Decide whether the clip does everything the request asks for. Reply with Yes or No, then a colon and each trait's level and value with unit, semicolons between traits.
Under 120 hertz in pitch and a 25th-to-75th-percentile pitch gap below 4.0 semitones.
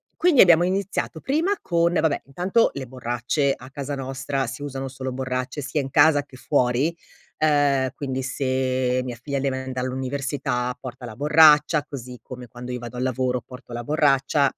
No: low, 135 Hz; narrow, 2.6 semitones